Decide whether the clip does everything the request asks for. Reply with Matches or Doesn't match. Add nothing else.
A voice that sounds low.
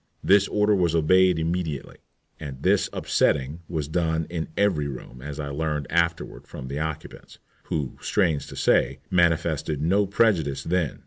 Matches